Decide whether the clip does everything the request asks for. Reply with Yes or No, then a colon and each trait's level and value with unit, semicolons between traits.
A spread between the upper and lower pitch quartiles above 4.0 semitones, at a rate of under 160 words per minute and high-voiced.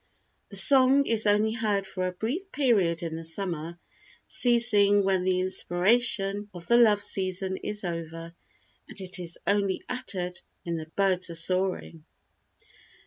No: average, 3.5 semitones; average, 145 wpm; high, 195 Hz